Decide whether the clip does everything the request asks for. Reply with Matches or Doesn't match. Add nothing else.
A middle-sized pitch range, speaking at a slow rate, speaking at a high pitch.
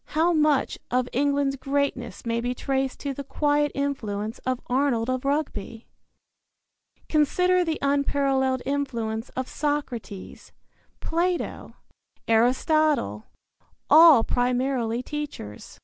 Matches